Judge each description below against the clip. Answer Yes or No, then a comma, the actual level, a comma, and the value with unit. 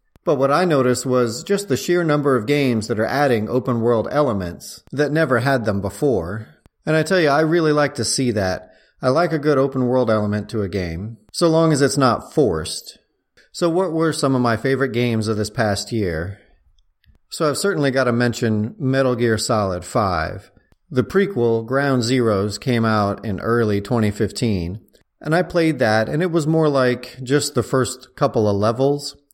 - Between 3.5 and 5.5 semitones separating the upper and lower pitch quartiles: Yes, average, 4.9 semitones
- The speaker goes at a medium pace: Yes, average, 190 wpm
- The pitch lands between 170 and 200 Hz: No, low, 125 Hz